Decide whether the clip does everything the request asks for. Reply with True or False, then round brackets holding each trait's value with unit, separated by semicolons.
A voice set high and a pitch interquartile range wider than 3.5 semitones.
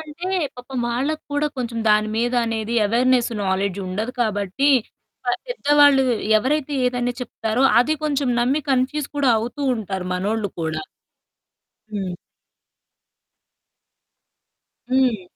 True (245 Hz; 4.5 semitones)